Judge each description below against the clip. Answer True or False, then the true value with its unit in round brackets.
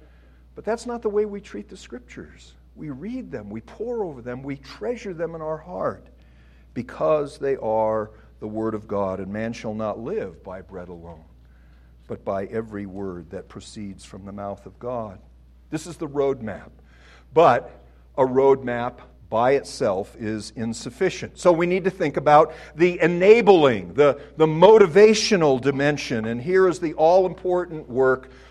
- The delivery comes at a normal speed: True (165 wpm)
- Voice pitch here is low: True (125 Hz)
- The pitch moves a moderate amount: False (8.8 semitones)